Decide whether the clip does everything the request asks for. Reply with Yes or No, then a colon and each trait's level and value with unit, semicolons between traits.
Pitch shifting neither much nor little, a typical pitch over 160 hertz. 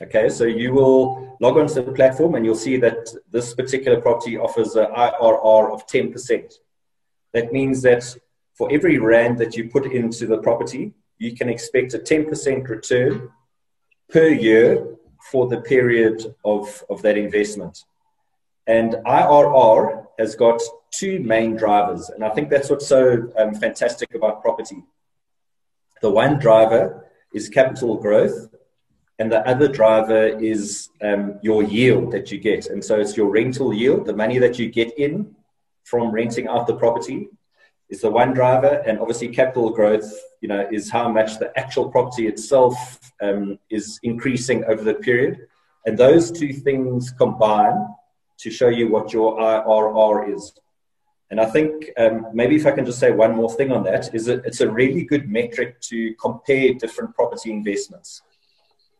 No: average, 3.2 semitones; low, 115 Hz